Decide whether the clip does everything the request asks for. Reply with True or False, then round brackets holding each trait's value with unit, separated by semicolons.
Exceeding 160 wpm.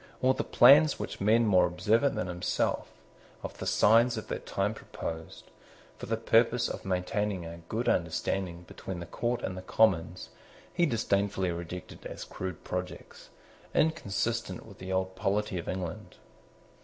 False (155 wpm)